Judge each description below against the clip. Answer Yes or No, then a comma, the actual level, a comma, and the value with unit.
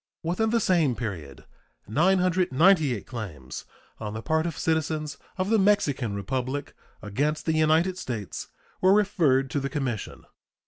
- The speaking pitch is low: No, medium, 150 Hz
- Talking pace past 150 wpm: No, slow, 135 wpm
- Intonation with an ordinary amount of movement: No, wide, 6.9 semitones